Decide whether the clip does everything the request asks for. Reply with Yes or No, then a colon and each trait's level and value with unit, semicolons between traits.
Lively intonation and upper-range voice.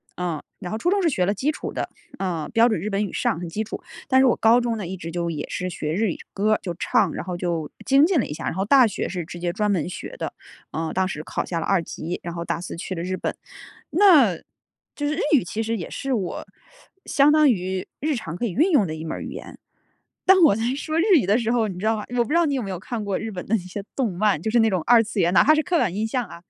Yes: wide, 5.7 semitones; high, 205 Hz